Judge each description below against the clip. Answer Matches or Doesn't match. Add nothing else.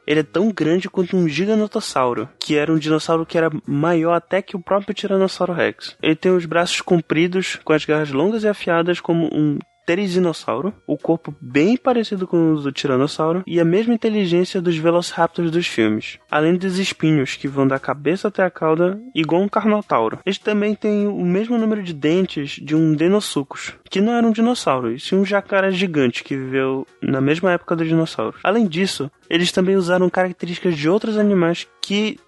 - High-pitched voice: Doesn't match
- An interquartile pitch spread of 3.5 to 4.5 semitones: Matches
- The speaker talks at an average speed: Doesn't match